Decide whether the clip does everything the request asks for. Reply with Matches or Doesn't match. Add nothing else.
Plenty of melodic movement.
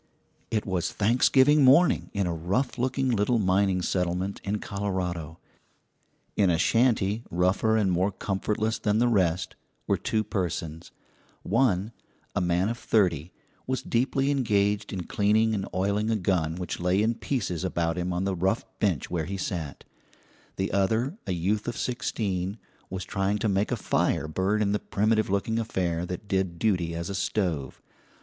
Doesn't match